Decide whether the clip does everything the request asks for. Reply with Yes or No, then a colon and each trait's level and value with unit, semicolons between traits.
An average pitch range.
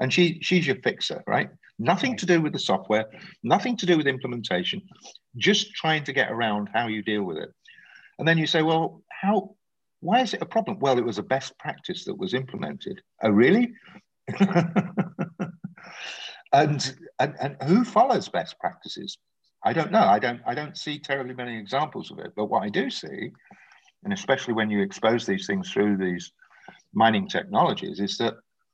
No: wide, 7.7 semitones